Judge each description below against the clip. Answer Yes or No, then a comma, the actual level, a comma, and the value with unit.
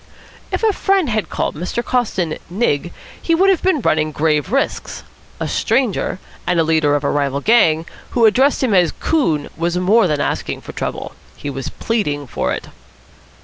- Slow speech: No, average, 180 wpm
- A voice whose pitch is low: No, medium, 180 Hz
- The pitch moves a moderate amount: No, wide, 8.0 semitones